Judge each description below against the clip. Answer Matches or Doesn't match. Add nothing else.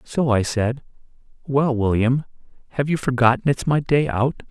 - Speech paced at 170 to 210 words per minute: Doesn't match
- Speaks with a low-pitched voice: Matches